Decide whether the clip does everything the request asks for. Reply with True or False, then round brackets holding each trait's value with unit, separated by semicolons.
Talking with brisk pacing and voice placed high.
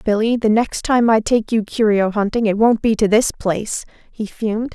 True (215 wpm; 220 Hz)